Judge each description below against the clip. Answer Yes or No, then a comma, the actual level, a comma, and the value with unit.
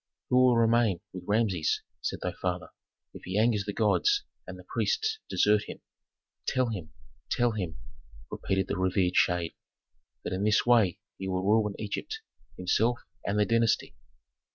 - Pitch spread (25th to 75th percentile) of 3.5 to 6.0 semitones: Yes, average, 3.8 semitones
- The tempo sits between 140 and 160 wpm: Yes, average, 155 wpm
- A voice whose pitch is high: No, low, 105 Hz